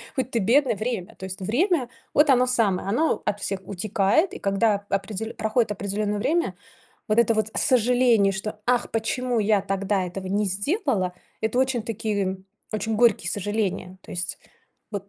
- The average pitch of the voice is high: Yes, high, 215 Hz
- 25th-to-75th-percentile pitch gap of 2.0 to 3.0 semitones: No, average, 3.8 semitones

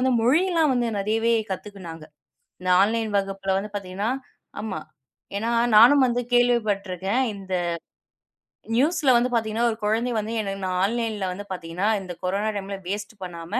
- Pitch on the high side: Yes, high, 210 Hz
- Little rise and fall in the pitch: No, average, 3.6 semitones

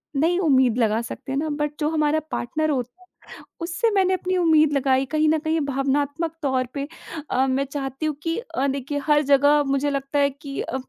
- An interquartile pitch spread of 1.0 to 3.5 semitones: Yes, narrow, 2.6 semitones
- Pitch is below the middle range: No, very high, 285 Hz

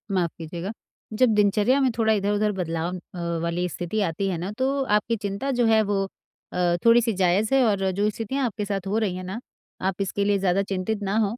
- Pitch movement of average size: Yes, average, 3.2 semitones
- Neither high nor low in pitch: No, high, 200 Hz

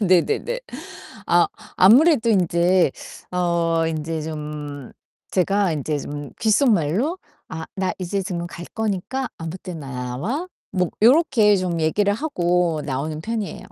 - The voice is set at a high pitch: No, medium, 180 Hz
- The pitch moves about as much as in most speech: Yes, average, 4.8 semitones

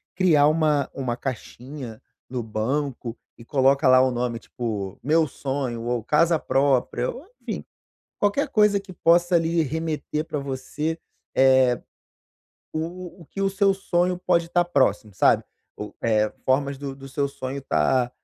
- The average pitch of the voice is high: No, medium, 140 Hz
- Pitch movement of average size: Yes, average, 4.9 semitones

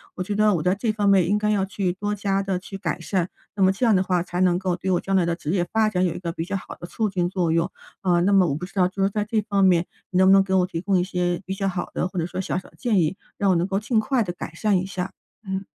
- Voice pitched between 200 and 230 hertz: No, high, 190 Hz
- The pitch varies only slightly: Yes, narrow, 1.9 semitones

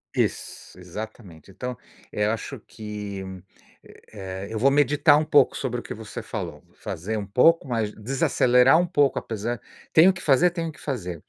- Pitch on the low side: Yes, low, 115 Hz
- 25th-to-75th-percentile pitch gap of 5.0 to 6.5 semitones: Yes, wide, 5.6 semitones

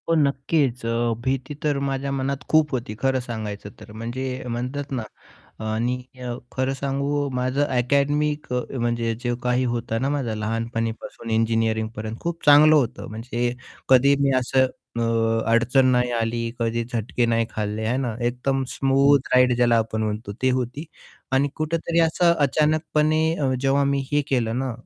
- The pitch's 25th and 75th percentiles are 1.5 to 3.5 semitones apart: Yes, average, 3.2 semitones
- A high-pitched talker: No, low, 125 Hz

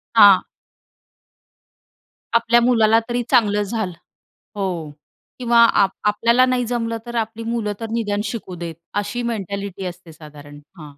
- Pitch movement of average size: Yes, average, 3.6 semitones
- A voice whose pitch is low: No, high, 215 Hz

